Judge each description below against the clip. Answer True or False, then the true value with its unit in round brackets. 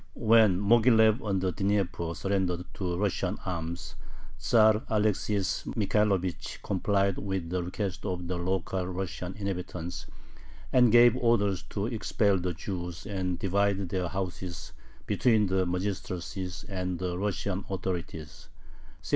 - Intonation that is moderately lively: False (2.3 semitones)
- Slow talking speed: True (125 wpm)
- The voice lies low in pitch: True (95 Hz)